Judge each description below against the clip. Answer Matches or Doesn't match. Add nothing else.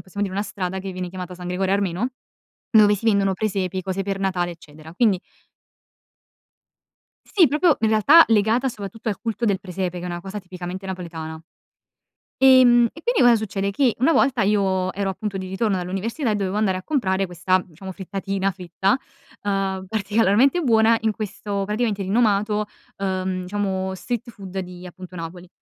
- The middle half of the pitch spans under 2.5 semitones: Doesn't match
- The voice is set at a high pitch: Matches